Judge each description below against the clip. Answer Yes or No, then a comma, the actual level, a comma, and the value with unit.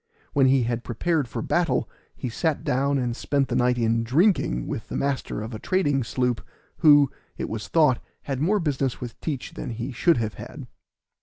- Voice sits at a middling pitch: No, low, 130 Hz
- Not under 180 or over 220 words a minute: Yes, average, 190 wpm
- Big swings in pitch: No, average, 3.6 semitones